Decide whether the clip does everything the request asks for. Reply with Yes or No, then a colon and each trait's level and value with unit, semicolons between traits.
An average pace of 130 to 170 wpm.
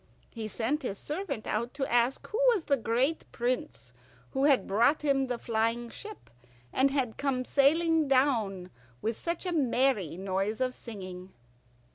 Yes: average, 155 wpm